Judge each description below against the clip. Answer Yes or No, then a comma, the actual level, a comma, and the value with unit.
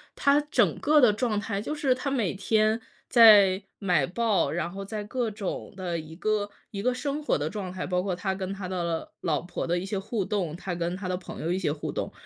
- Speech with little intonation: No, average, 3.5 semitones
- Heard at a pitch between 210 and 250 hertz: No, high, 195 Hz